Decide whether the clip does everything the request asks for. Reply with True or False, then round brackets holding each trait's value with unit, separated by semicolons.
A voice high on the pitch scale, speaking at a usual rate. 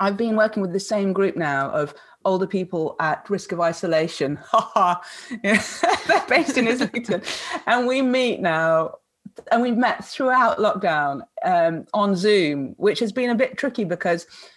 True (210 Hz; 160 wpm)